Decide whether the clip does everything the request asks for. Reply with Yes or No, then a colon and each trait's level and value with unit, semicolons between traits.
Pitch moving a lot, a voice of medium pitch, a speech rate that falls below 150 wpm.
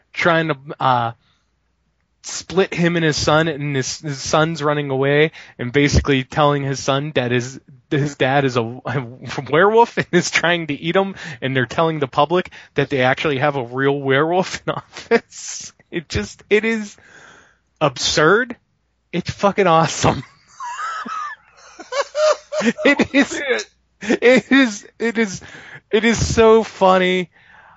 Yes: wide, 6.4 semitones; medium, 160 Hz; average, 140 wpm